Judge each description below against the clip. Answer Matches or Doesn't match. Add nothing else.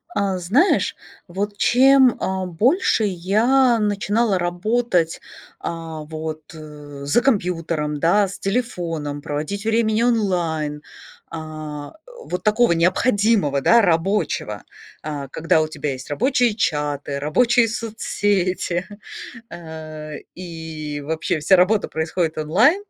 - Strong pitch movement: Matches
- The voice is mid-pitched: Matches